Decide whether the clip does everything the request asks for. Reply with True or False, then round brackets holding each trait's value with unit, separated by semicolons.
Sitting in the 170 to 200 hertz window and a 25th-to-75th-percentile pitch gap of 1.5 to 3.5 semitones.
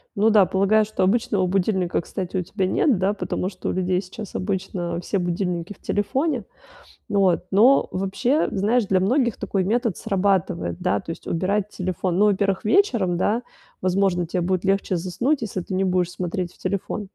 True (190 Hz; 2.4 semitones)